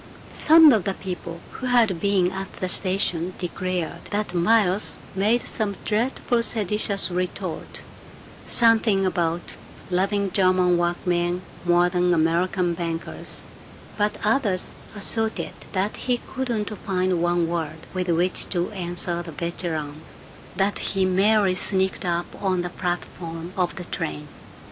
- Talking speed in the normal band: No, slow, 130 wpm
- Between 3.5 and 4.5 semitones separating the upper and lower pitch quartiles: No, average, 2.8 semitones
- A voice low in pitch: No, medium, 185 Hz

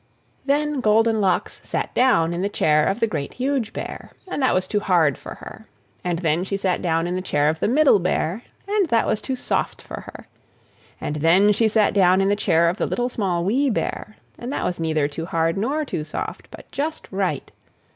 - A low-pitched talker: No, high, 195 Hz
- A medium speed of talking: No, fast, 215 wpm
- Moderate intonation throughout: No, wide, 5.9 semitones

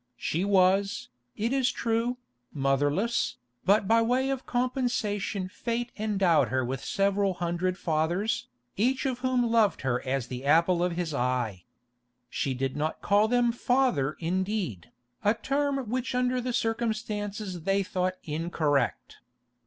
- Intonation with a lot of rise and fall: Yes, wide, 6.8 semitones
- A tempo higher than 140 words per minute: No, slow, 135 wpm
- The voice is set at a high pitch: Yes, high, 200 Hz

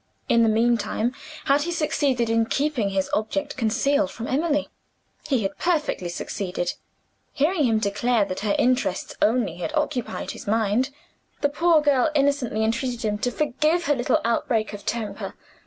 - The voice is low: No, high, 245 Hz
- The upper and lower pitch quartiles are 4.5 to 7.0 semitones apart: Yes, average, 5.0 semitones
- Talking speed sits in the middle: Yes, average, 155 wpm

